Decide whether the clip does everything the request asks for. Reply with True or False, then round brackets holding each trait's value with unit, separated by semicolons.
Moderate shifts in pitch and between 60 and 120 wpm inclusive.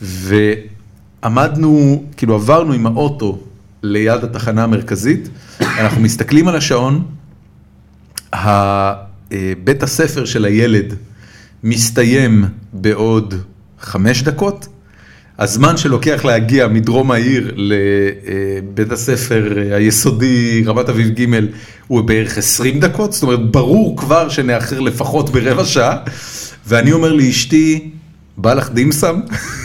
True (4.8 semitones; 100 wpm)